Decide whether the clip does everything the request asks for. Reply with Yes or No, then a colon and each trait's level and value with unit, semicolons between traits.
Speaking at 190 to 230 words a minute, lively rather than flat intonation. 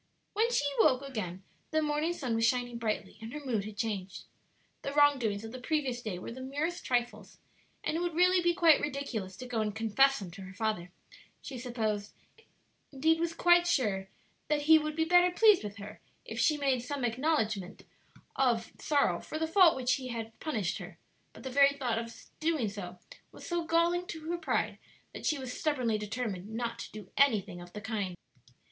Yes: average, 200 wpm; wide, 6.1 semitones